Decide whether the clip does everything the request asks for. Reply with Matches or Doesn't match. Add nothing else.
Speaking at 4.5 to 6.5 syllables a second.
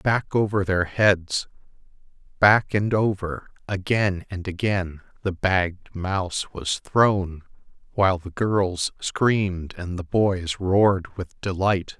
Doesn't match